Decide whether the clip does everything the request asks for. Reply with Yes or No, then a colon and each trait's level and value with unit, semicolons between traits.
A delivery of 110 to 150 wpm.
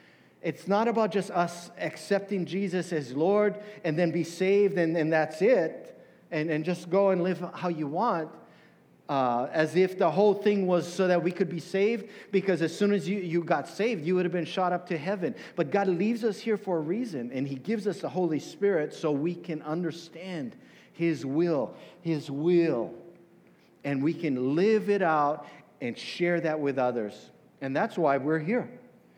No: average, 195 wpm